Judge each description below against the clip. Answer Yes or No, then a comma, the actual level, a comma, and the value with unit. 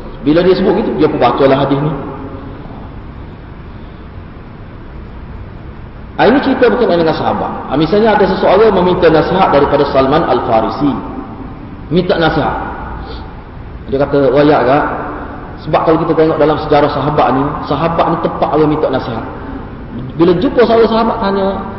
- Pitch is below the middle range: No, medium, 150 Hz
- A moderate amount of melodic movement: Yes, average, 4.3 semitones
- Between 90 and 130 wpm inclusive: No, average, 145 wpm